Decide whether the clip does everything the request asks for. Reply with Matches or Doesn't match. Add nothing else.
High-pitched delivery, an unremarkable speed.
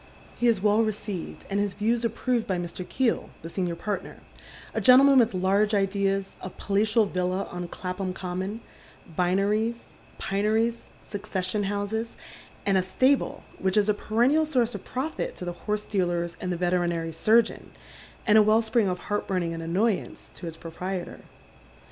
Matches